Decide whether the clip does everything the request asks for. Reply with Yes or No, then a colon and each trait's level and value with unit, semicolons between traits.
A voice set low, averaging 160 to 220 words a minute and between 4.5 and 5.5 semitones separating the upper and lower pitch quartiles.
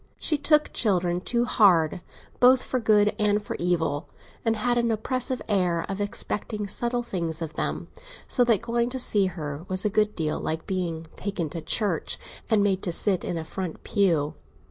No: high, 200 Hz; average, 185 wpm; average, 5.1 semitones